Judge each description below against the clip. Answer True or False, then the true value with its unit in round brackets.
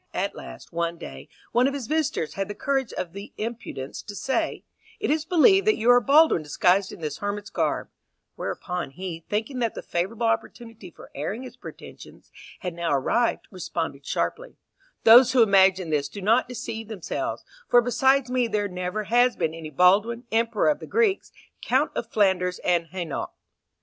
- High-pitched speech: True (210 Hz)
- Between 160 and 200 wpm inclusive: True (175 wpm)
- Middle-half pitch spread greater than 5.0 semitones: True (5.5 semitones)